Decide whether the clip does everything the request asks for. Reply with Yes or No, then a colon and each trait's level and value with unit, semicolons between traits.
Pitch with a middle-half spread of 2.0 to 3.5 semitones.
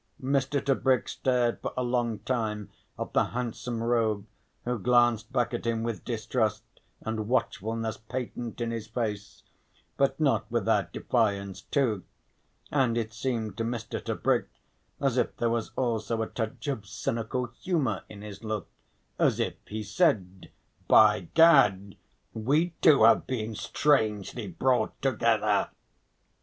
Yes: narrow, 2.6 semitones